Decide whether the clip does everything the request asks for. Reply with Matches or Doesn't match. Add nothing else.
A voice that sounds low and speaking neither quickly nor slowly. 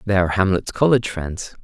Matches